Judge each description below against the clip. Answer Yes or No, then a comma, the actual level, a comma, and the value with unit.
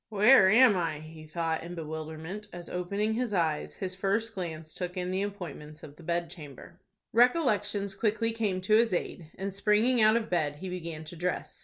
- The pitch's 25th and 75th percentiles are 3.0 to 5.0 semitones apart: Yes, average, 4.4 semitones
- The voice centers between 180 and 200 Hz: Yes, medium, 185 Hz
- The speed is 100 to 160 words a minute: No, average, 185 wpm